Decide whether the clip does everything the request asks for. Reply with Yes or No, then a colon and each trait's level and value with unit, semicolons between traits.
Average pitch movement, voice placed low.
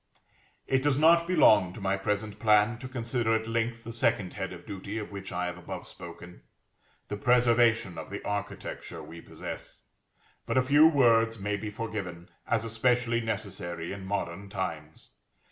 Yes: average, 3.5 semitones; low, 110 Hz